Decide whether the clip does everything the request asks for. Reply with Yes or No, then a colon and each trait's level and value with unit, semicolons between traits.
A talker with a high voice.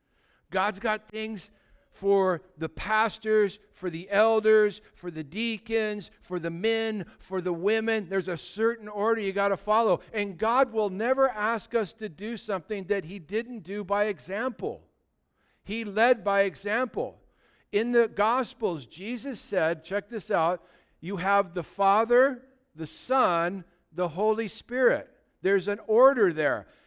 Yes: high, 210 Hz